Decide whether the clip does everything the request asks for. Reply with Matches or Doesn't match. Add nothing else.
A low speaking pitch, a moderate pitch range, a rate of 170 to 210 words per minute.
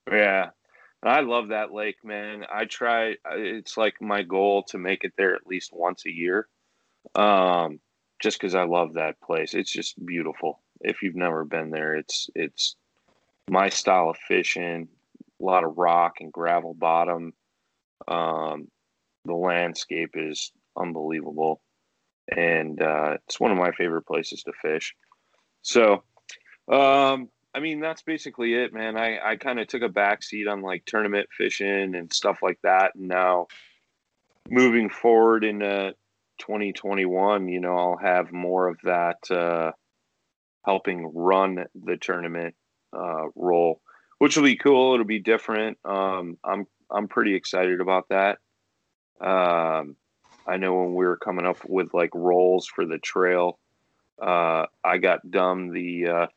Doesn't match